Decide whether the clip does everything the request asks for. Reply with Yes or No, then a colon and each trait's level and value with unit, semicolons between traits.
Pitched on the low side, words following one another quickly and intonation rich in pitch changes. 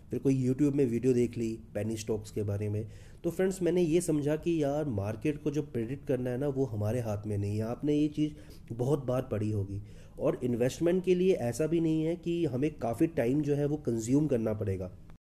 Yes: low, 125 Hz; fast, 225 wpm; wide, 5.9 semitones